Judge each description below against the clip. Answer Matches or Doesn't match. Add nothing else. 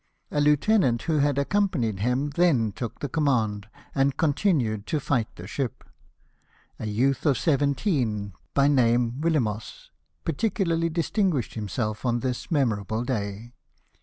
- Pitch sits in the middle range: Doesn't match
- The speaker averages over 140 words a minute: Doesn't match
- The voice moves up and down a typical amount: Matches